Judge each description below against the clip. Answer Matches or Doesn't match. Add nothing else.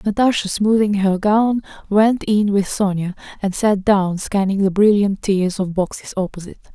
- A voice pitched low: Doesn't match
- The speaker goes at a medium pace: Matches